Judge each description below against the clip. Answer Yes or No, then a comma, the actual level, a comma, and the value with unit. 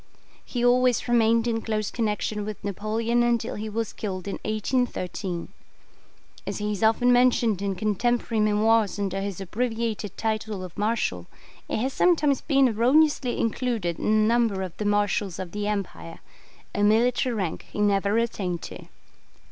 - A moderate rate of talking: Yes, average, 155 wpm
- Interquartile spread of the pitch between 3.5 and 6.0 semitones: No, average, 2.8 semitones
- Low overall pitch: No, high, 215 Hz